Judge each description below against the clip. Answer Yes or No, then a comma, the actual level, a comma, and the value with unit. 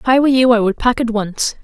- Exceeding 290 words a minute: Yes, fast, 330 wpm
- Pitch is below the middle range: No, high, 235 Hz